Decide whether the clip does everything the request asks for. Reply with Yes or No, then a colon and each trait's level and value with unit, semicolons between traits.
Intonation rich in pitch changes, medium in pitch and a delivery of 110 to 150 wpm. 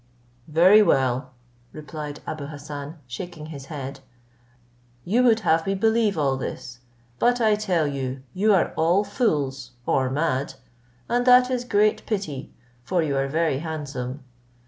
Yes: wide, 7.0 semitones; medium, 155 Hz; average, 145 wpm